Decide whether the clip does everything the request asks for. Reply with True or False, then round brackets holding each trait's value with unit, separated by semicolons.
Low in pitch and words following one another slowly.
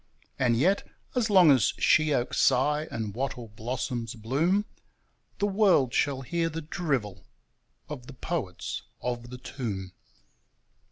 True (130 Hz; 125 wpm)